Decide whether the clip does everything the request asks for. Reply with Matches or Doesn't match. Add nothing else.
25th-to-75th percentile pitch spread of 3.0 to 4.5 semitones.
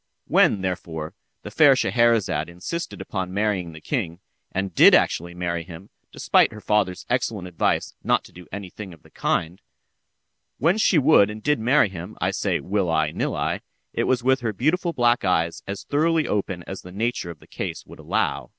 Doesn't match